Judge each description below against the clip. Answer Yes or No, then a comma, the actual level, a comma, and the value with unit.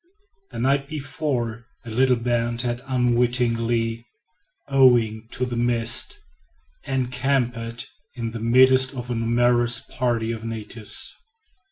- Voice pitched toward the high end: No, low, 120 Hz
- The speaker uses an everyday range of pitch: No, narrow, 1.7 semitones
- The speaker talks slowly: Yes, slow, 115 wpm